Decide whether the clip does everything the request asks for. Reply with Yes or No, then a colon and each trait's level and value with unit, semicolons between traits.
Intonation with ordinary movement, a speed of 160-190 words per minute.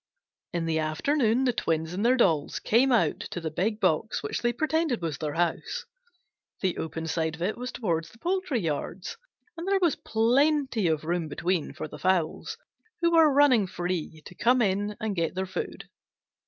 No: wide, 7.5 semitones; average, 185 wpm